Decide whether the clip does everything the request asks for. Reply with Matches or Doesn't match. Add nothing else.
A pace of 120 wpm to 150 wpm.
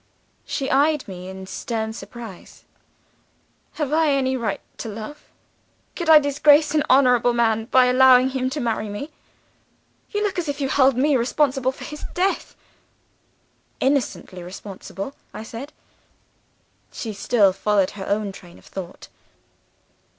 Matches